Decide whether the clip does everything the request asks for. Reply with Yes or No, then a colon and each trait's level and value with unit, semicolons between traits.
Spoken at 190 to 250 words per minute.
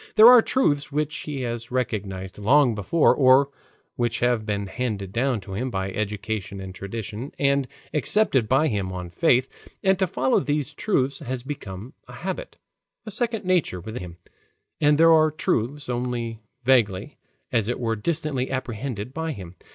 No: average, 165 wpm